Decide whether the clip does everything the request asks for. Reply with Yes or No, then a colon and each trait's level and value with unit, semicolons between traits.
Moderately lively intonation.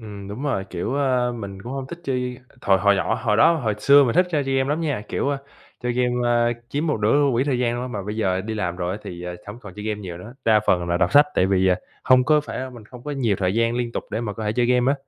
Yes: average, 4.4 semitones